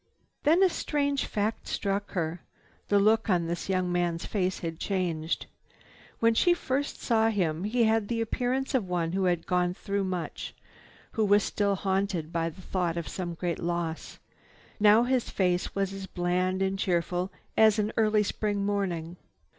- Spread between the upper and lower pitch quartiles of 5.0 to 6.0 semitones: No, average, 3.6 semitones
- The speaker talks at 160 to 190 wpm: Yes, average, 165 wpm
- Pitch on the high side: Yes, high, 195 Hz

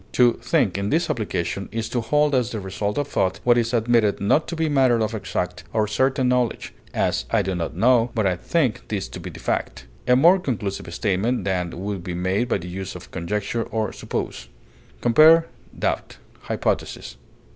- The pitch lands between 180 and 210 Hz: No, low, 110 Hz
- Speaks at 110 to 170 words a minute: No, average, 190 wpm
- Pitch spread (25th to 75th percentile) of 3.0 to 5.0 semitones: Yes, average, 4.6 semitones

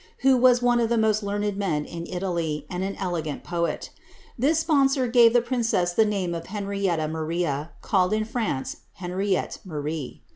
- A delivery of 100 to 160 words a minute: No, average, 170 wpm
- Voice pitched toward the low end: No, high, 195 Hz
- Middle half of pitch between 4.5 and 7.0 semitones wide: Yes, average, 5.3 semitones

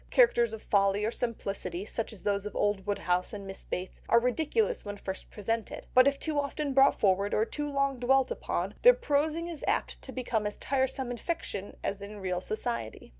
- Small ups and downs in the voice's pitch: No, wide, 5.6 semitones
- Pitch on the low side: No, high, 230 Hz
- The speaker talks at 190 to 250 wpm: Yes, average, 200 wpm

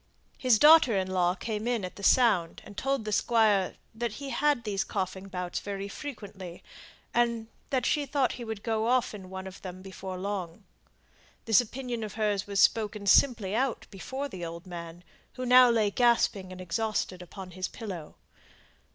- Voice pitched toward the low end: No, high, 210 Hz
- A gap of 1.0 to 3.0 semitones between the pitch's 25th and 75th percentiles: No, average, 4.2 semitones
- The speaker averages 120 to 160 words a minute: No, average, 175 wpm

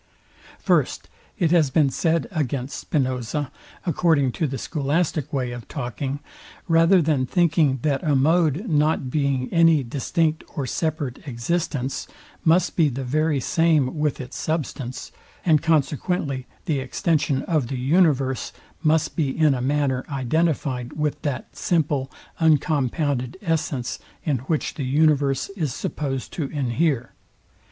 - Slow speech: Yes, slow, 130 wpm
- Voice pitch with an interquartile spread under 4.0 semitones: Yes, average, 3.5 semitones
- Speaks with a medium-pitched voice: Yes, medium, 145 Hz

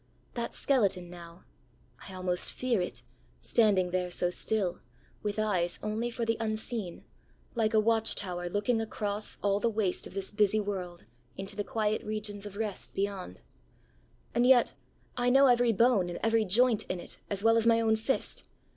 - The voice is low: No, high, 210 Hz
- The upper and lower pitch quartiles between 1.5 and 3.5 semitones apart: Yes, average, 3.2 semitones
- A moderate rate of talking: Yes, average, 170 wpm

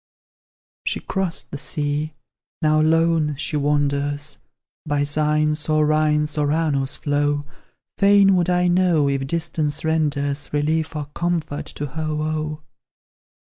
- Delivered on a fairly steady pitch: Yes, narrow, 1.7 semitones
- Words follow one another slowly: Yes, slow, 125 wpm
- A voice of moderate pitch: Yes, medium, 150 Hz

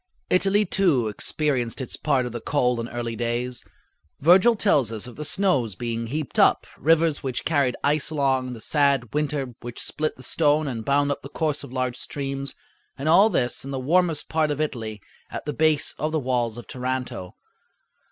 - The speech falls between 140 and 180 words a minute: No, average, 190 wpm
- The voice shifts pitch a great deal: No, average, 4.0 semitones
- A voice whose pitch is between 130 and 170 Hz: Yes, medium, 140 Hz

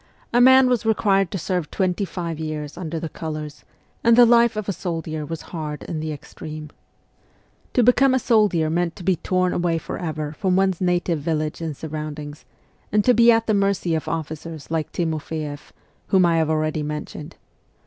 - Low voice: No, medium, 165 Hz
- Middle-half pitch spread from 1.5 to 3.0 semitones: No, average, 4.1 semitones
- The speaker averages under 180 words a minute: No, average, 185 wpm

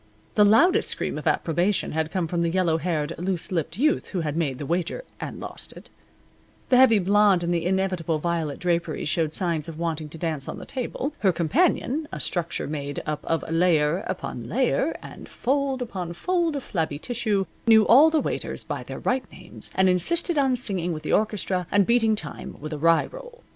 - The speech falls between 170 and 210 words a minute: Yes, average, 200 wpm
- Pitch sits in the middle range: Yes, medium, 180 Hz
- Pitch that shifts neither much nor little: No, wide, 5.8 semitones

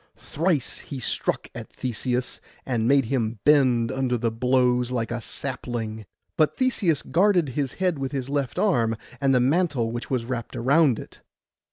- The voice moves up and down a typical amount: Yes, average, 3.4 semitones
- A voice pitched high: No, low, 130 Hz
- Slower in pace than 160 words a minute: No, average, 165 wpm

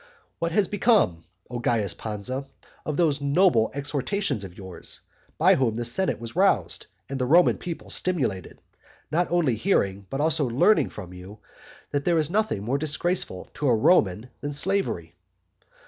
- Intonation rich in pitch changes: Yes, wide, 8.4 semitones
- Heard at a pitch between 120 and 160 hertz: Yes, medium, 140 Hz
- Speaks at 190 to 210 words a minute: No, average, 160 wpm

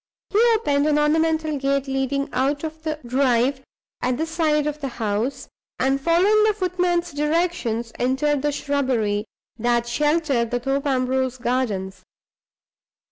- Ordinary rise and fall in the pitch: Yes, average, 3.8 semitones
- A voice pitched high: Yes, very high, 275 Hz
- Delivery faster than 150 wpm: No, slow, 135 wpm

